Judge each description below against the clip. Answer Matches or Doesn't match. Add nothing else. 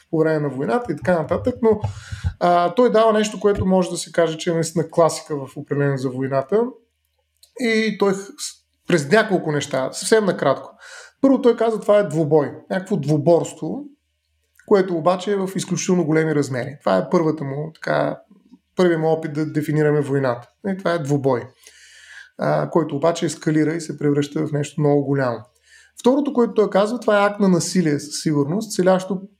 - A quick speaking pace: Matches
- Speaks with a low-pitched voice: Doesn't match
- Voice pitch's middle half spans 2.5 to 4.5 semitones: Doesn't match